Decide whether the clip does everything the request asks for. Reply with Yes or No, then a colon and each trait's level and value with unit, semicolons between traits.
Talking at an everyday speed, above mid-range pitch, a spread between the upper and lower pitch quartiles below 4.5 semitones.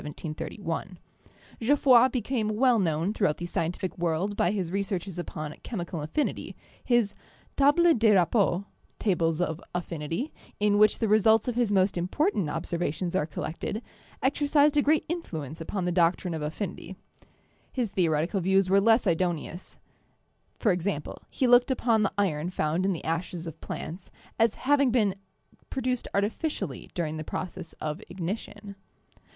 No: average, 150 wpm; high, 195 Hz; average, 5.2 semitones